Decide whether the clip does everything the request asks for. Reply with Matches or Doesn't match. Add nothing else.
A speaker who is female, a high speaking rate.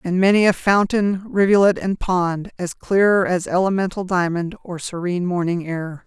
Doesn't match